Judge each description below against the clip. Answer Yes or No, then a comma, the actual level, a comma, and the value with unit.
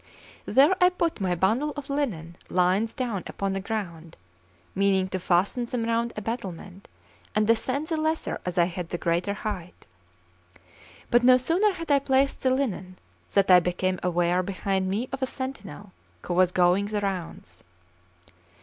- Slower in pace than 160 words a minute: No, average, 165 wpm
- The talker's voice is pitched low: No, high, 200 Hz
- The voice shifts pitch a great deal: Yes, wide, 5.9 semitones